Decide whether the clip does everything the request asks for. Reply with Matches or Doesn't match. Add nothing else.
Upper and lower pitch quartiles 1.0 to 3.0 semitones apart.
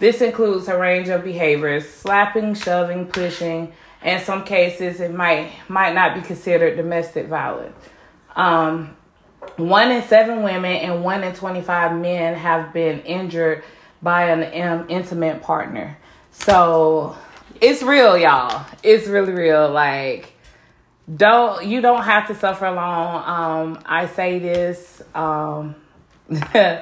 Matches